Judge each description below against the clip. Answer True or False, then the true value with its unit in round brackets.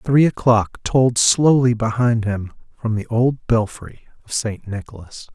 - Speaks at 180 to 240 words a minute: False (145 wpm)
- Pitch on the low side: True (115 Hz)